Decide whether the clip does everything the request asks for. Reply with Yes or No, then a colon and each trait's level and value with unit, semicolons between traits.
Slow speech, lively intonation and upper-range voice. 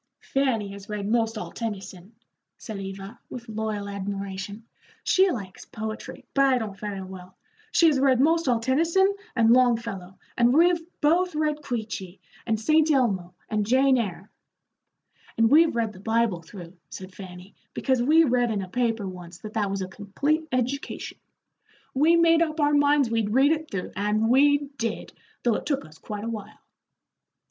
No: average, 170 wpm; wide, 5.7 semitones; high, 225 Hz